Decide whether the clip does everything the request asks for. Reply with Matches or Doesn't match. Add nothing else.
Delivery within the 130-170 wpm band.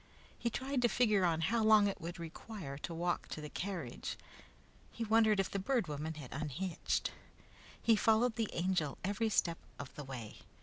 Doesn't match